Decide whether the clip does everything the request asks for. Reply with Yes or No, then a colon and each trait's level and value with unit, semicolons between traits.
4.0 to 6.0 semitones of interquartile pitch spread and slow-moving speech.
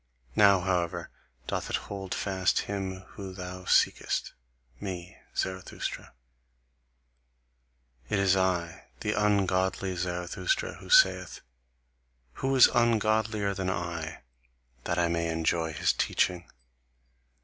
No: narrow, 2.4 semitones; slow, 105 wpm